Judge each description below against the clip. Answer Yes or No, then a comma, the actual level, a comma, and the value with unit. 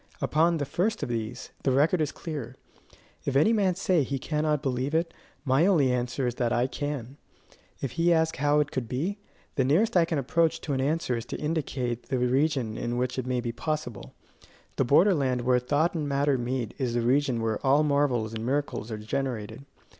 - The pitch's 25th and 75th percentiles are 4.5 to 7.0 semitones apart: No, average, 3.9 semitones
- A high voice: No, low, 135 Hz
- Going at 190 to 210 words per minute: Yes, fast, 205 wpm